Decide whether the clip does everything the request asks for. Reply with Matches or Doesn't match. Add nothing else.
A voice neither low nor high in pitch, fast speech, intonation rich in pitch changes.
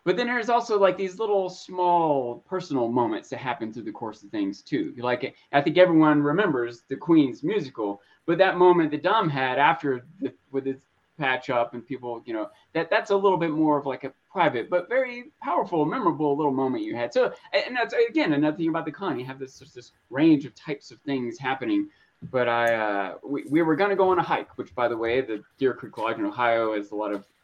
Matches